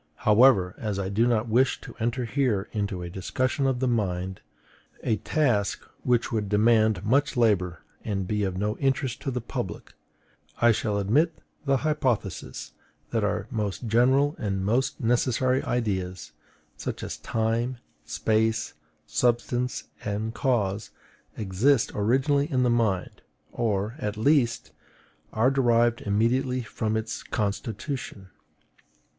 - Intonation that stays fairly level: No, average, 3.7 semitones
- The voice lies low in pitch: Yes, low, 115 Hz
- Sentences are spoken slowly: Yes, slow, 130 wpm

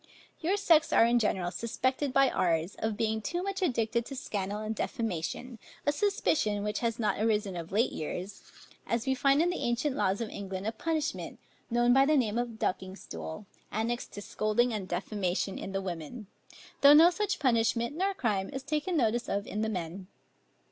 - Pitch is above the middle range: Yes, high, 230 Hz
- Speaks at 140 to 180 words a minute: No, average, 190 wpm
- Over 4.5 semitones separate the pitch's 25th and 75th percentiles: Yes, average, 5.2 semitones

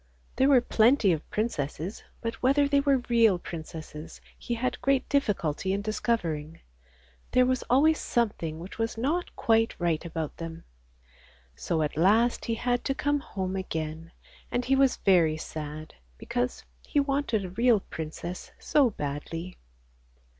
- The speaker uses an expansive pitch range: Yes, wide, 7.4 semitones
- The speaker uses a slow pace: No, average, 145 wpm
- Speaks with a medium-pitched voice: No, high, 215 Hz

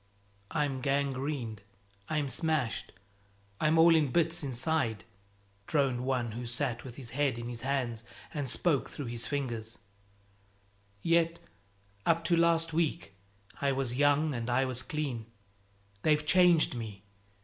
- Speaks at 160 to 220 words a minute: No, slow, 135 wpm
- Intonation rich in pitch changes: No, average, 4.5 semitones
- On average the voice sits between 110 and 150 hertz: Yes, medium, 140 Hz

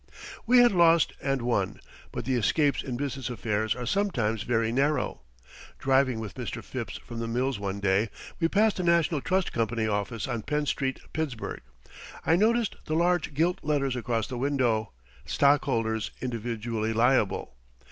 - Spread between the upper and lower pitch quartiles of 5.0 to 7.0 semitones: Yes, average, 5.3 semitones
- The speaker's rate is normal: Yes, average, 155 wpm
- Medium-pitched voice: No, low, 130 Hz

